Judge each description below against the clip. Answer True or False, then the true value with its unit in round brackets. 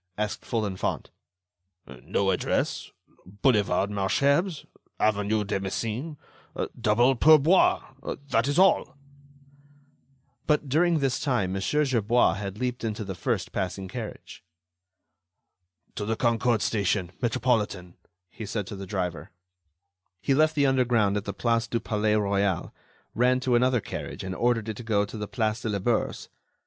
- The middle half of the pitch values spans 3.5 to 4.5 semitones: True (4.0 semitones)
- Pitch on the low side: True (110 Hz)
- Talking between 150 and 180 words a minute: False (140 wpm)